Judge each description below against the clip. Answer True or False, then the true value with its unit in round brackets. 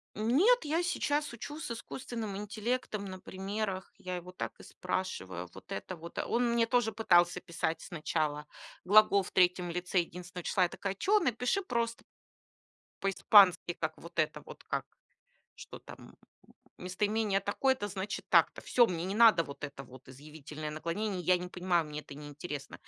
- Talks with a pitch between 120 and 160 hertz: False (185 Hz)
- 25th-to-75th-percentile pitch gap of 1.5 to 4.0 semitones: False (4.7 semitones)